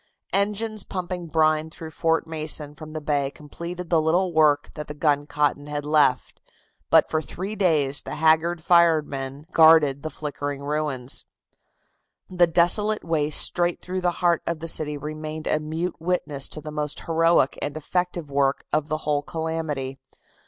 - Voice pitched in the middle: Yes, medium, 155 Hz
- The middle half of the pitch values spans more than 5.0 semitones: No, narrow, 2.5 semitones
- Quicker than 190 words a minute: No, average, 160 wpm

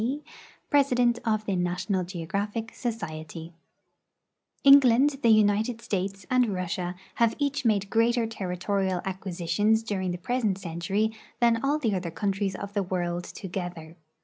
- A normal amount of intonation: Yes, average, 4.2 semitones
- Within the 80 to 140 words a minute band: Yes, slow, 135 wpm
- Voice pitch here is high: Yes, high, 200 Hz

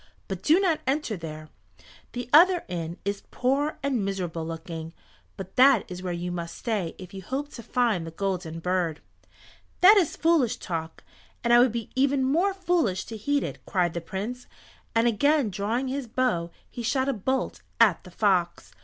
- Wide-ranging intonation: Yes, wide, 7.1 semitones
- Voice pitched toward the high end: Yes, high, 220 Hz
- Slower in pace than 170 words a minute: No, average, 180 wpm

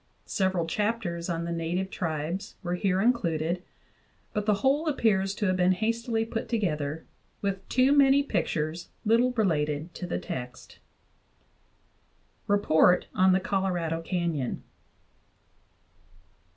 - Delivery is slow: Yes, slow, 120 wpm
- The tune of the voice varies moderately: Yes, average, 4.6 semitones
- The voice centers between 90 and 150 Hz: No, medium, 185 Hz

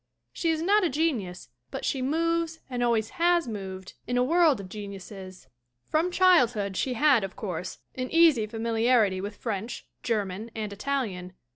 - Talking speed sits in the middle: Yes, average, 165 wpm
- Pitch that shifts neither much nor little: No, wide, 7.7 semitones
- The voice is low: No, high, 230 Hz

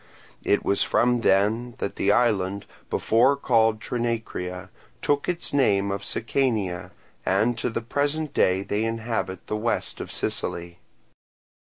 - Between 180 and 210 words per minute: No, slow, 135 wpm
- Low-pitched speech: Yes, low, 115 Hz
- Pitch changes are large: No, average, 3.7 semitones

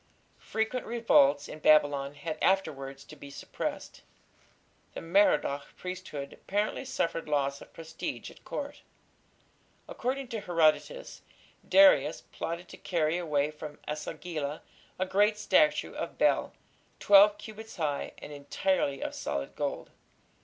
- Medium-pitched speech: Yes, medium, 165 Hz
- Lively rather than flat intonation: Yes, wide, 6.0 semitones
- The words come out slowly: Yes, slow, 125 wpm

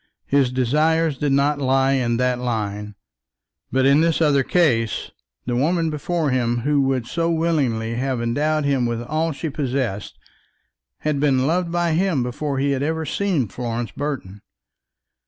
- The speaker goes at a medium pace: Yes, average, 160 wpm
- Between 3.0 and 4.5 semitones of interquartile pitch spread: Yes, average, 4.2 semitones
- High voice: No, low, 135 Hz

